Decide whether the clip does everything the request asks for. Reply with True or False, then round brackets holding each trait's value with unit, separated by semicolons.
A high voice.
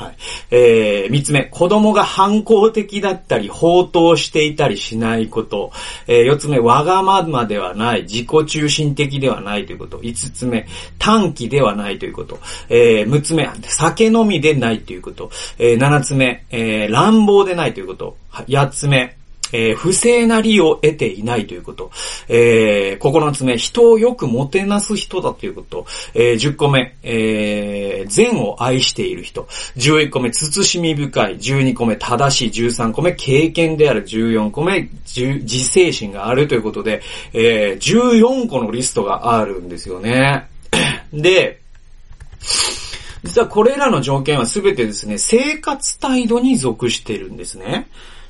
False (140 Hz)